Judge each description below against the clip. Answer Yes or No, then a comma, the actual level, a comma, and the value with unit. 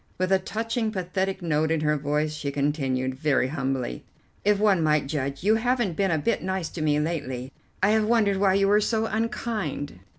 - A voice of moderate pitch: Yes, medium, 170 Hz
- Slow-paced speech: No, average, 195 wpm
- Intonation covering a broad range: Yes, wide, 6.0 semitones